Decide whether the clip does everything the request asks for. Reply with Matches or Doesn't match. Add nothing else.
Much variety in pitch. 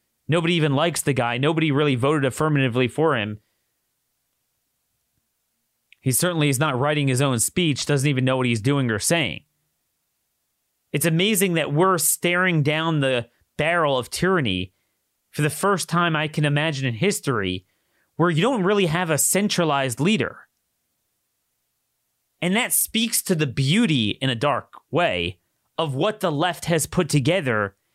Doesn't match